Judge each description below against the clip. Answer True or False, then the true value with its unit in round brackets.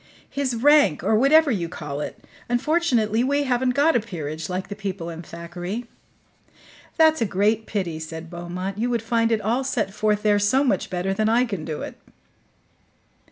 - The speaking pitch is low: False (215 Hz)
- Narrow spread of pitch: False (5.6 semitones)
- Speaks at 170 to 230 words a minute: True (180 wpm)